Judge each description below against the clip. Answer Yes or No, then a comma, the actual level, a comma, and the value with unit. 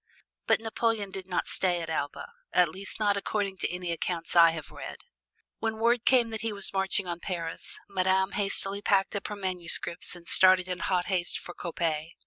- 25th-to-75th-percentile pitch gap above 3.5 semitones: No, narrow, 2.6 semitones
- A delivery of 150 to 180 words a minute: No, average, 190 wpm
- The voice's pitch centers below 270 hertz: Yes, high, 190 Hz